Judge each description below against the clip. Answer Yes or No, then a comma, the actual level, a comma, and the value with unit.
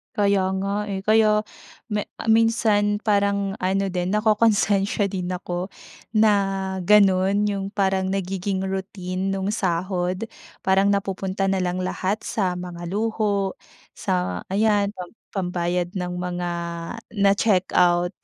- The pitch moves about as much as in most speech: No, narrow, 2.1 semitones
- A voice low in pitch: No, high, 195 Hz